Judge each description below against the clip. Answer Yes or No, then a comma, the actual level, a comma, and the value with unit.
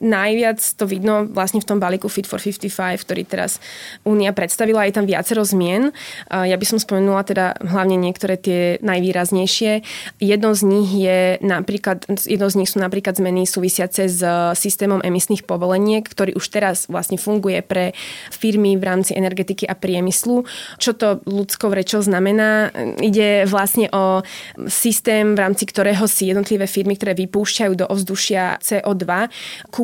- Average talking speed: Yes, average, 150 wpm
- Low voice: No, high, 195 Hz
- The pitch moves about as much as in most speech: No, narrow, 2.0 semitones